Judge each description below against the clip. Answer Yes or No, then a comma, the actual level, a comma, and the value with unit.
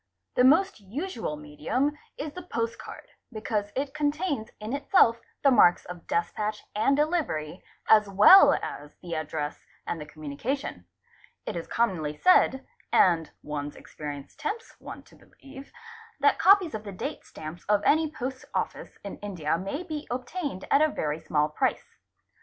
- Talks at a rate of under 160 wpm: Yes, average, 150 wpm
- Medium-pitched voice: No, high, 215 Hz